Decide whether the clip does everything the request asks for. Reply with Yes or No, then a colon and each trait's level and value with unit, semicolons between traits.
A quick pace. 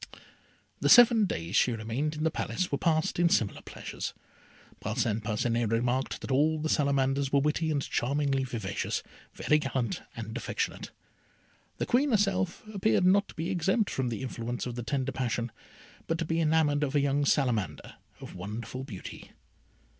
No: average, 165 wpm